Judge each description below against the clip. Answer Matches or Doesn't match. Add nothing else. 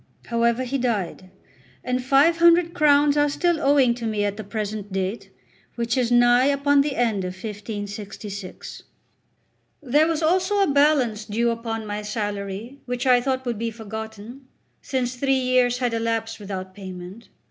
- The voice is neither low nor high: Doesn't match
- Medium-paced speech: Matches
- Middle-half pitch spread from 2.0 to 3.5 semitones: Doesn't match